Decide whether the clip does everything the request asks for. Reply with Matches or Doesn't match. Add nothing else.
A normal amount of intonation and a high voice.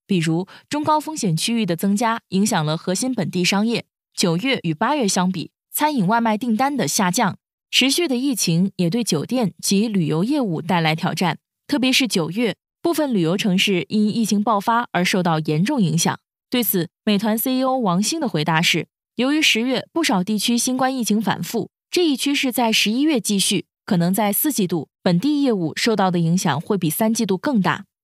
Doesn't match